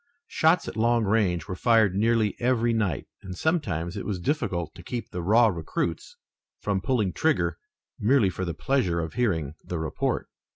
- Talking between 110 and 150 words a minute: No, average, 170 wpm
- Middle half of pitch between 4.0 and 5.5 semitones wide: Yes, average, 5.1 semitones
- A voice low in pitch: Yes, low, 105 Hz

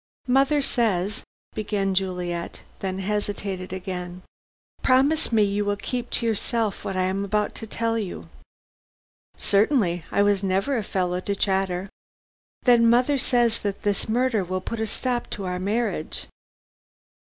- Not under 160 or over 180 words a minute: No, average, 150 wpm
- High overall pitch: Yes, high, 205 Hz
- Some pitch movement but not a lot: Yes, average, 3.7 semitones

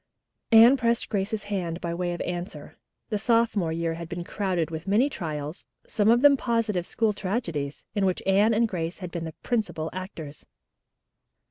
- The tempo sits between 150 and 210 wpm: Yes, average, 170 wpm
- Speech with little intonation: No, average, 4.8 semitones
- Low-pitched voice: No, high, 190 Hz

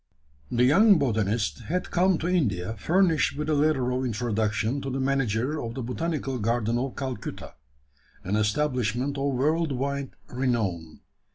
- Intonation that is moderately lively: Yes, average, 4.7 semitones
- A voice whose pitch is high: No, low, 130 Hz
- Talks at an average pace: Yes, average, 150 wpm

